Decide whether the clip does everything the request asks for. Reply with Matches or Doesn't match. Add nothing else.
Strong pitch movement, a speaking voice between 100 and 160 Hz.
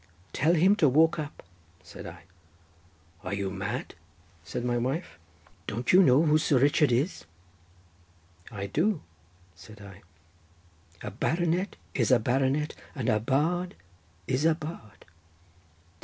Matches